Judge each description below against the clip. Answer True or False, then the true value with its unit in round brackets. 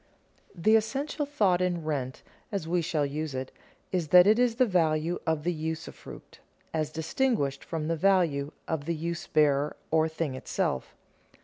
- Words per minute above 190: False (165 wpm)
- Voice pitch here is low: False (160 Hz)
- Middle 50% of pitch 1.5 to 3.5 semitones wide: True (3.1 semitones)